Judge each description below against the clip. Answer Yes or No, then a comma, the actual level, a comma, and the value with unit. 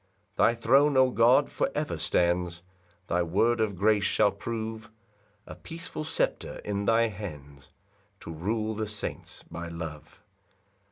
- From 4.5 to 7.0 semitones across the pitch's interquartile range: Yes, average, 4.9 semitones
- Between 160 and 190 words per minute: No, average, 145 wpm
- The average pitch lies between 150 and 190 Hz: No, low, 105 Hz